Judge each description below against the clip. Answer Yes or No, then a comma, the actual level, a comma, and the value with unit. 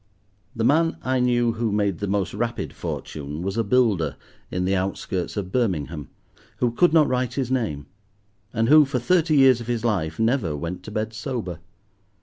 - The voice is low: Yes, low, 110 Hz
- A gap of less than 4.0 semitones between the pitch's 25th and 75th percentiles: No, wide, 5.5 semitones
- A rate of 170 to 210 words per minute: Yes, average, 180 wpm